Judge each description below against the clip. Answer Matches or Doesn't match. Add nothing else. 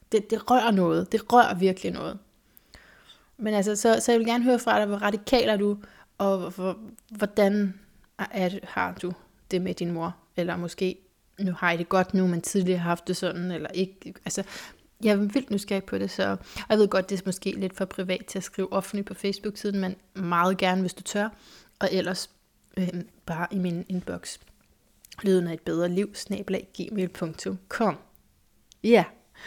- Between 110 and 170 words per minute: Doesn't match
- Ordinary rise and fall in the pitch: Doesn't match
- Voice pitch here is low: Doesn't match